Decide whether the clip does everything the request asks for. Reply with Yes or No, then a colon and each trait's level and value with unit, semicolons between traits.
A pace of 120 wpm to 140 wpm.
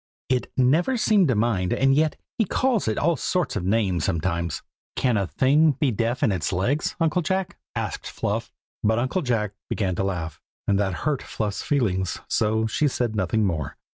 No: average, 185 wpm